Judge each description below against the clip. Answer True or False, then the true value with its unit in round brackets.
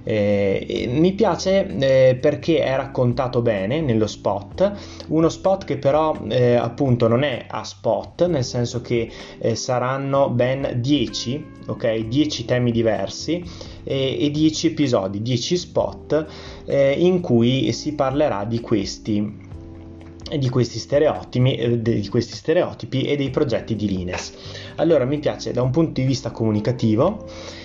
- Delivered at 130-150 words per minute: True (140 wpm)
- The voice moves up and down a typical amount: True (4.7 semitones)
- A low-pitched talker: True (125 Hz)